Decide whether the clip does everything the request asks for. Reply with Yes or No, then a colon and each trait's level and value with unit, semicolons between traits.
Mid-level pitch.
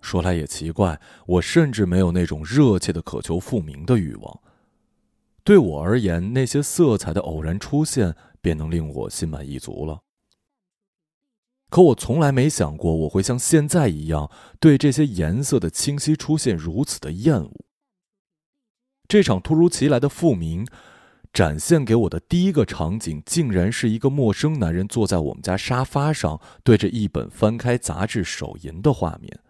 No: low, 115 Hz